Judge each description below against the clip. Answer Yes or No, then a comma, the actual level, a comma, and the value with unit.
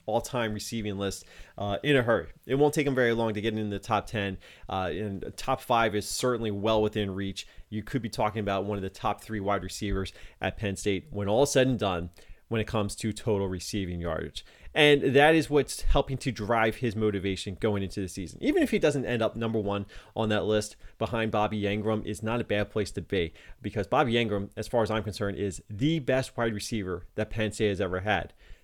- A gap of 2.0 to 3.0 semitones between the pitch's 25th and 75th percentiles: Yes, average, 2.7 semitones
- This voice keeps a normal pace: No, fast, 225 wpm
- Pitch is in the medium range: No, low, 105 Hz